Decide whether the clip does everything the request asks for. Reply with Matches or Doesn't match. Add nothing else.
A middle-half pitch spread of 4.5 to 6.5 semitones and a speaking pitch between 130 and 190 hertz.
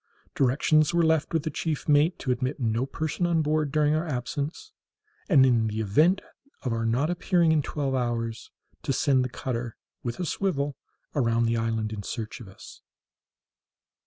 Matches